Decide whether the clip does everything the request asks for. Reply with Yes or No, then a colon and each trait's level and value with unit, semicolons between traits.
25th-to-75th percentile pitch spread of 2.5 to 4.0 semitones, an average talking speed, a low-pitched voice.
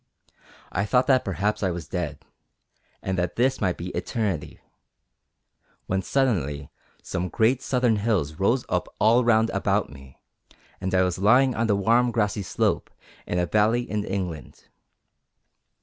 No: average, 4.7 semitones; average, 150 wpm; low, 100 Hz